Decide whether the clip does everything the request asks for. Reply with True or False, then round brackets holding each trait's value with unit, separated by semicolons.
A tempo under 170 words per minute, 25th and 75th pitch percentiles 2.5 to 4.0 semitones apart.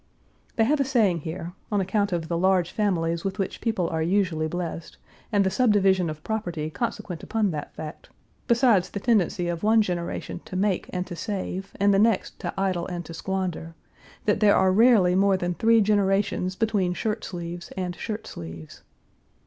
False (180 wpm; 3.3 semitones)